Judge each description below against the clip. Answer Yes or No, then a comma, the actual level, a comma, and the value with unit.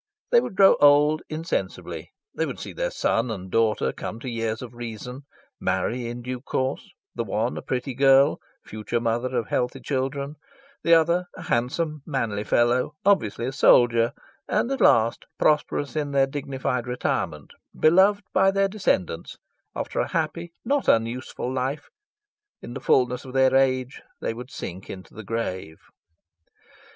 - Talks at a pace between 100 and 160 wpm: Yes, average, 155 wpm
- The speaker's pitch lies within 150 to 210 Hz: No, low, 130 Hz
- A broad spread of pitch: No, average, 4.2 semitones